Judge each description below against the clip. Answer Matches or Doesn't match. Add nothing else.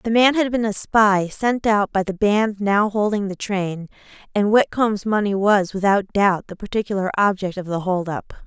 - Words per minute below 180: Doesn't match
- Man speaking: Doesn't match